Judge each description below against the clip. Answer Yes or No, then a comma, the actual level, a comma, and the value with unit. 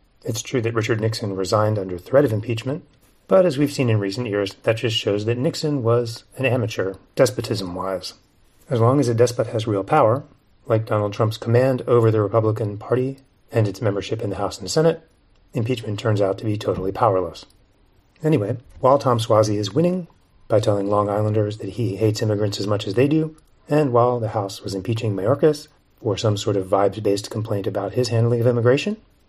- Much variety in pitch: No, average, 3.7 semitones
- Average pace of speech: Yes, average, 195 wpm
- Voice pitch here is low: Yes, low, 110 Hz